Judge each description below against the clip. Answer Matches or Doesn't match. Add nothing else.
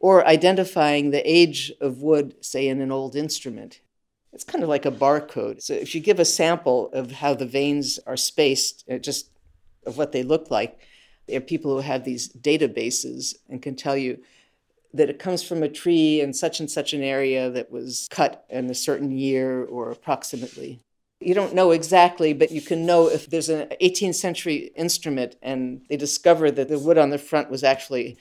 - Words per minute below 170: Doesn't match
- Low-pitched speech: Doesn't match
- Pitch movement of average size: Matches